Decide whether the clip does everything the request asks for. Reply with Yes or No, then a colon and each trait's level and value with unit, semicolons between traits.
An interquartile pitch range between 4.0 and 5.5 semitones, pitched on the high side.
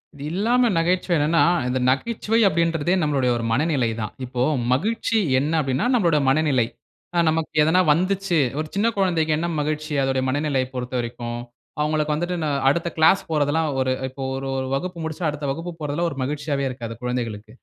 No: average, 4.4 semitones; medium, 150 Hz